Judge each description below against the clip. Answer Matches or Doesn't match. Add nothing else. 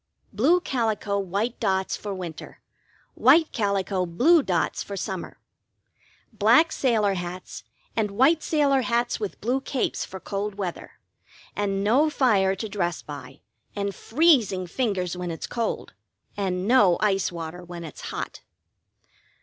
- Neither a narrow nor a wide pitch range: Matches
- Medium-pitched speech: Doesn't match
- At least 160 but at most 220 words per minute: Doesn't match